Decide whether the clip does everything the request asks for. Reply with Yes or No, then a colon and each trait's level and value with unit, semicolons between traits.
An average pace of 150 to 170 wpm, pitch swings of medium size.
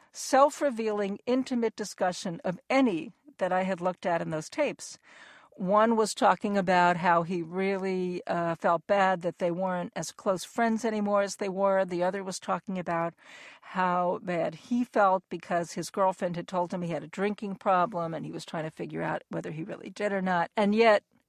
No: average, 195 wpm; average, 3.0 semitones